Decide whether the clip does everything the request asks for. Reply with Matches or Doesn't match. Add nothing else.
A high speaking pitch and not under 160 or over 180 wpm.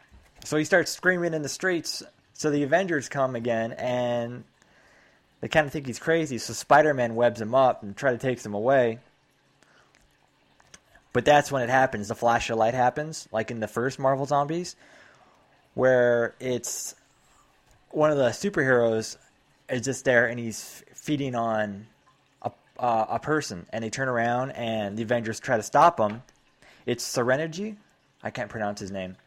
Doesn't match